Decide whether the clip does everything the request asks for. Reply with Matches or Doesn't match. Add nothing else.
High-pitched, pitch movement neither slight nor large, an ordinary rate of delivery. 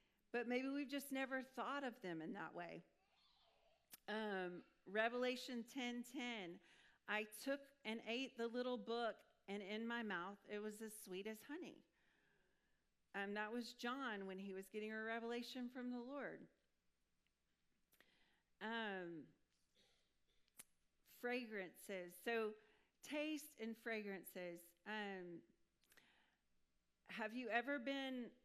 Doesn't match